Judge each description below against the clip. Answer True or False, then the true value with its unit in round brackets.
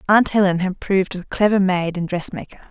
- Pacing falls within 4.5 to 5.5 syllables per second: False (5.9 syllables/s)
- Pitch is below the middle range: False (190 Hz)